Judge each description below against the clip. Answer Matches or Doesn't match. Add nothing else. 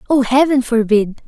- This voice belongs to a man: Doesn't match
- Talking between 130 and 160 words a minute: Matches